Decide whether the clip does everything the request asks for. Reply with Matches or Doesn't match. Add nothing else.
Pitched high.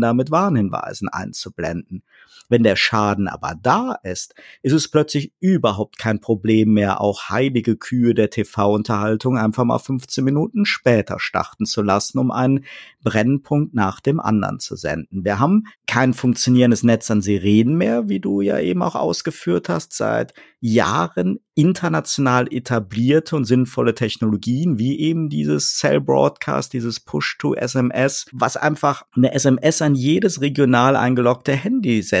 Doesn't match